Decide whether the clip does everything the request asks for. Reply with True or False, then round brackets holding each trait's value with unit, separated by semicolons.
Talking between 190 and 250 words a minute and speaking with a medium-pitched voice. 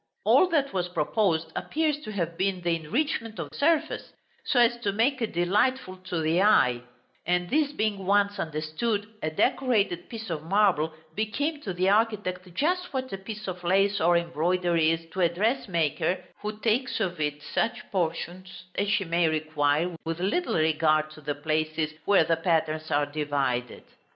False (170 wpm; 180 Hz)